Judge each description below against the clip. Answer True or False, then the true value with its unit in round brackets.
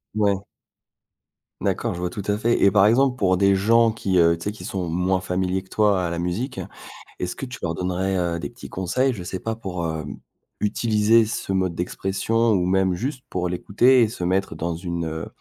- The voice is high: False (95 Hz)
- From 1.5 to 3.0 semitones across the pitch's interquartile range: False (3.7 semitones)